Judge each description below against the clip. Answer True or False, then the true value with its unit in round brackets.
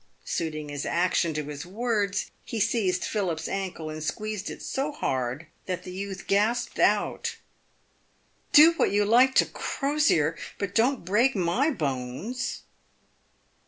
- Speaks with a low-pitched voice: False (195 Hz)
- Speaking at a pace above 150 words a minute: False (140 wpm)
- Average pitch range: False (6.3 semitones)